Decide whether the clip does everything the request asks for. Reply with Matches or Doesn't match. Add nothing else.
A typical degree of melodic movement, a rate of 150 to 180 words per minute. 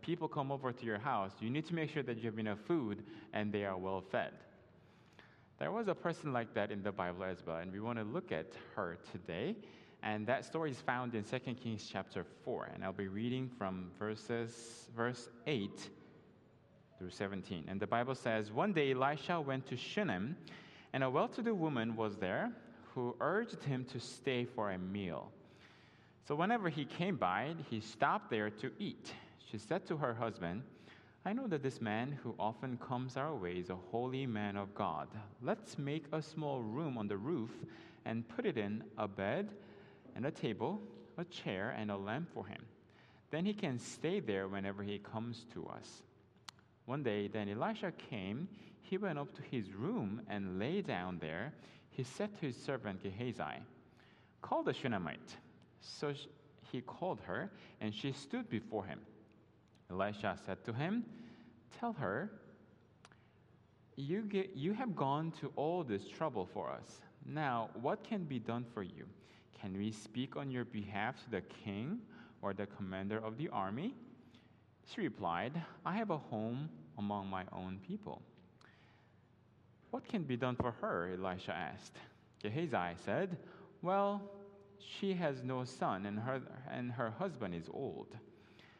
Doesn't match